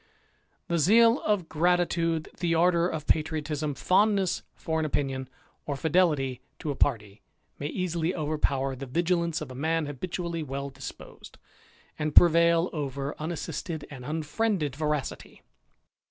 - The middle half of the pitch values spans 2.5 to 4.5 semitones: Yes, average, 3.2 semitones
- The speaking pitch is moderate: Yes, medium, 160 Hz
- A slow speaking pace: Yes, slow, 130 wpm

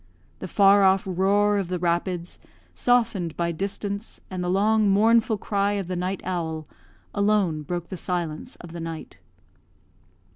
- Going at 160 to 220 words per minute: No, average, 150 wpm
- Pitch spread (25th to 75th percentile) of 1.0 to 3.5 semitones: Yes, average, 2.8 semitones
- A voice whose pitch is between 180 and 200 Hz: Yes, high, 190 Hz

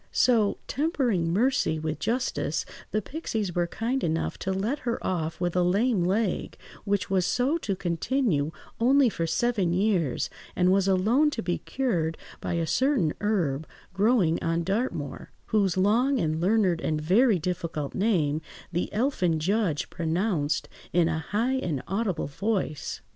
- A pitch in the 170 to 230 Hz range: Yes, high, 190 Hz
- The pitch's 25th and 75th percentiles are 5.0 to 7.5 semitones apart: Yes, wide, 5.6 semitones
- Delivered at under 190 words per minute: Yes, average, 150 wpm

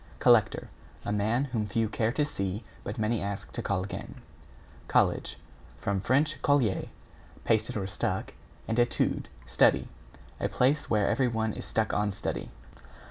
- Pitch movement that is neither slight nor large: Yes, average, 3.0 semitones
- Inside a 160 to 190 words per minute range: No, average, 145 wpm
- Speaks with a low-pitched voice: Yes, low, 110 Hz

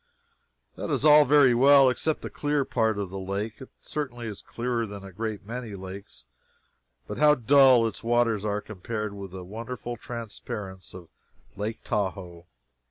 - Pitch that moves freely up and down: No, average, 3.9 semitones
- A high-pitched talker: No, low, 110 Hz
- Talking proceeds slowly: No, average, 165 wpm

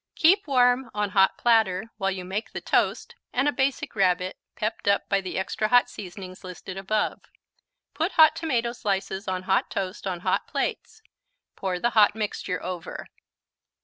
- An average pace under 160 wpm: No, average, 165 wpm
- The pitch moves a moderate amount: Yes, average, 4.3 semitones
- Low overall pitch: No, high, 200 Hz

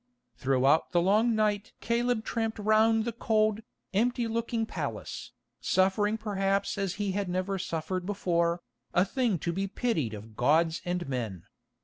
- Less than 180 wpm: Yes, average, 145 wpm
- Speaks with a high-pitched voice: Yes, high, 195 Hz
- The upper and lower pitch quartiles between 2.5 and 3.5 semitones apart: No, average, 4.4 semitones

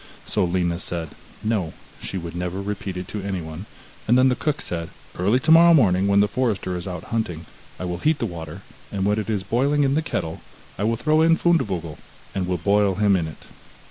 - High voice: No, low, 100 Hz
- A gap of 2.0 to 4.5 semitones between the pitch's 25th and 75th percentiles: No, average, 5.2 semitones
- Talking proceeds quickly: Yes, fast, 210 wpm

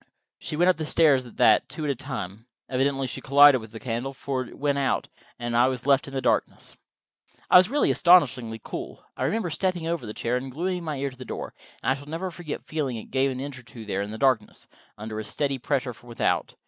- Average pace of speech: No, fast, 240 wpm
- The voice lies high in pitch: No, low, 135 Hz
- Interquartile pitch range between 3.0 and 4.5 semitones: Yes, average, 3.8 semitones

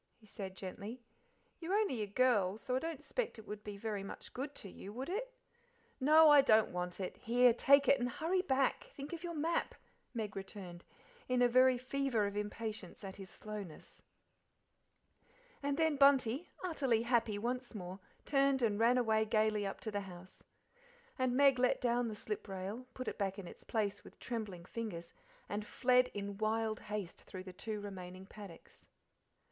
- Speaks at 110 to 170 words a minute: No, average, 180 wpm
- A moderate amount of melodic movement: Yes, average, 4.3 semitones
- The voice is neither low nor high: No, high, 225 Hz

